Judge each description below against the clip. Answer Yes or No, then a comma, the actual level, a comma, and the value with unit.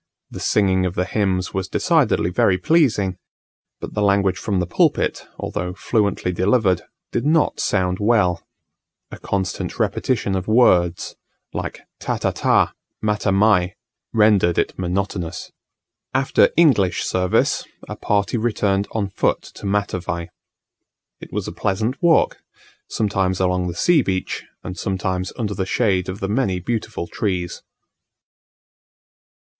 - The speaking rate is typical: No, slow, 130 wpm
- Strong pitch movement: No, narrow, 2.6 semitones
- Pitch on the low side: Yes, very low, 95 Hz